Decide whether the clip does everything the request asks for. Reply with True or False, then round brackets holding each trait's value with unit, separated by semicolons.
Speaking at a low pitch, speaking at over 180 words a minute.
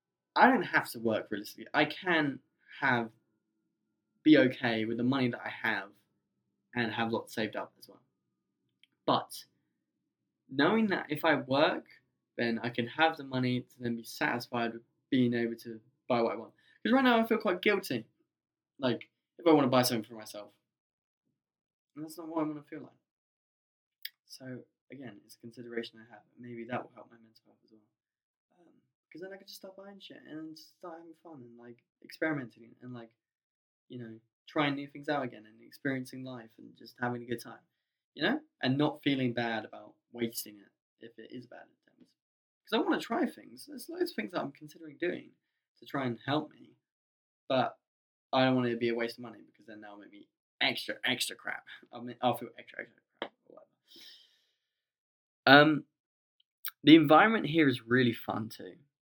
True (125 Hz; 190 wpm)